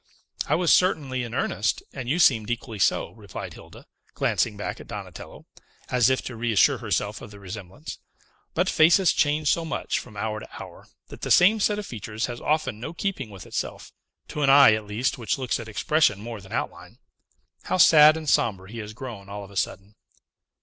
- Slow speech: No, average, 200 wpm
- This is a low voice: Yes, low, 120 Hz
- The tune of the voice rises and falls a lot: Yes, wide, 6.3 semitones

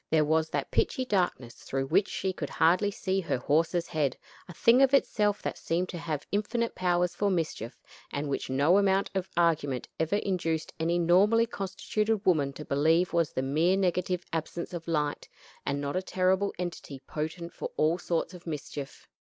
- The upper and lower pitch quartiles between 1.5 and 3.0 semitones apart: No, average, 3.8 semitones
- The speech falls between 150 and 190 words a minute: Yes, average, 180 wpm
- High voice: No, medium, 170 Hz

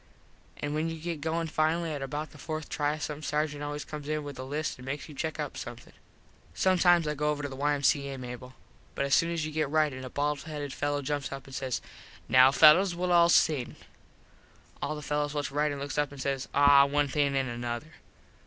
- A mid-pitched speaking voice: Yes, medium, 145 Hz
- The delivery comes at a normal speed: No, fast, 220 wpm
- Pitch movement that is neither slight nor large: No, narrow, 2.0 semitones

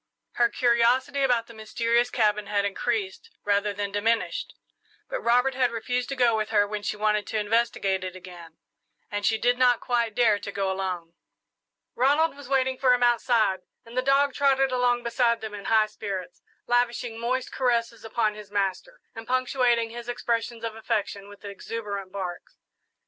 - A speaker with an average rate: Yes, average, 170 wpm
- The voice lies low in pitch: No, high, 230 Hz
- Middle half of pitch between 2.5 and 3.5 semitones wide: Yes, average, 3.2 semitones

